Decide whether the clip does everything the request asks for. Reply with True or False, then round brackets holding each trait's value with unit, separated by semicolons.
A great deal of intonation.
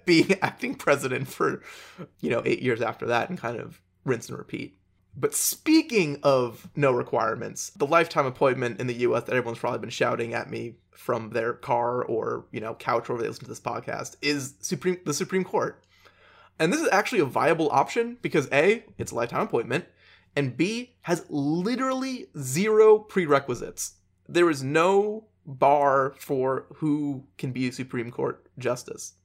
True (6.9 semitones)